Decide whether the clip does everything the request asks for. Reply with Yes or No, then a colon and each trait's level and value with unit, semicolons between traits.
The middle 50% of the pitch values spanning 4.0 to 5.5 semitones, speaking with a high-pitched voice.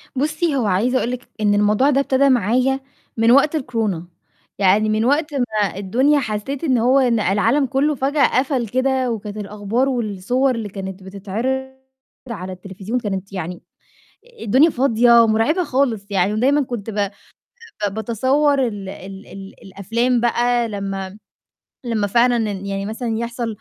Yes: average, 4.4 semitones; high, 230 Hz